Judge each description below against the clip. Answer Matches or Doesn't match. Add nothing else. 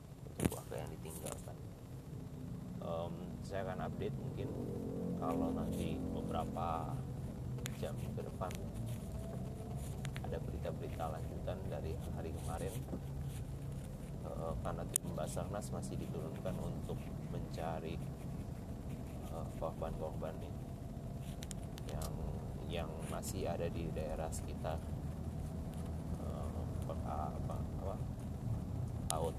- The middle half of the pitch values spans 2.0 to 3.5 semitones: Matches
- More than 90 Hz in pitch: Doesn't match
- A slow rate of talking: Matches